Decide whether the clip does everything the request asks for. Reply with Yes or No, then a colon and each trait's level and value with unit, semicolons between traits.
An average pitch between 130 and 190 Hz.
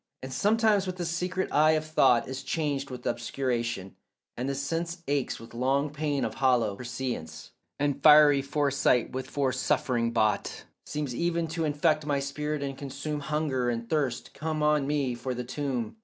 Yes: medium, 140 Hz